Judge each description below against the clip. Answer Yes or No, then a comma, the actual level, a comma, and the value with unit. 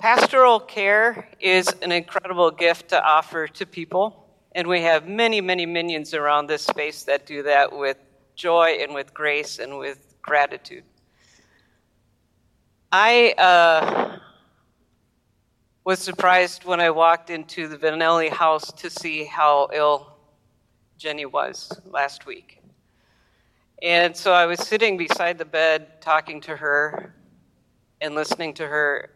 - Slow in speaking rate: Yes, slow, 130 wpm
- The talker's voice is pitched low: No, medium, 160 Hz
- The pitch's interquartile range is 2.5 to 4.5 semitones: Yes, average, 3.3 semitones